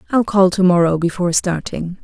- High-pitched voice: No, medium, 180 Hz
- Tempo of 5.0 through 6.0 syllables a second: Yes, 5.6 syllables/s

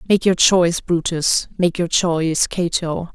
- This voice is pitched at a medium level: Yes, medium, 170 Hz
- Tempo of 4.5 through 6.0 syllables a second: No, 4.2 syllables/s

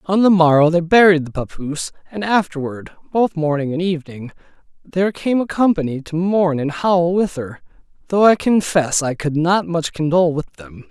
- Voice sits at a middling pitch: Yes, medium, 170 Hz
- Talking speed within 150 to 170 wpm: No, average, 180 wpm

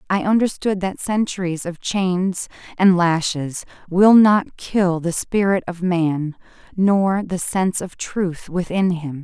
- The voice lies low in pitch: No, medium, 180 Hz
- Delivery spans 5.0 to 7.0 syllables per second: No, 3.7 syllables/s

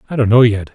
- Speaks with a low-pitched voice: Yes, low, 115 Hz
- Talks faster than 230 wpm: Yes, fast, 325 wpm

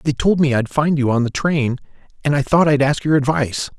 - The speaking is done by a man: Yes, male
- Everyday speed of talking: No, fast, 255 wpm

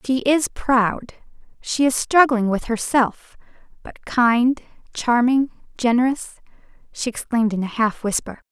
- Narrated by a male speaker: No, female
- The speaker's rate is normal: No, slow, 125 wpm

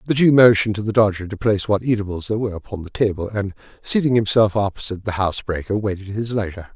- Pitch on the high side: No, low, 105 Hz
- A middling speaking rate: No, fast, 215 wpm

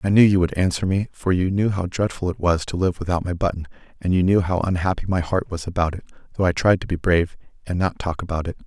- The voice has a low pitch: Yes, very low, 90 Hz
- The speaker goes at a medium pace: No, fast, 270 wpm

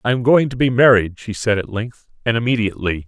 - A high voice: No, low, 115 Hz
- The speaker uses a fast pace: Yes, fast, 235 wpm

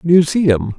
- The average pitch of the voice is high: No, medium, 150 Hz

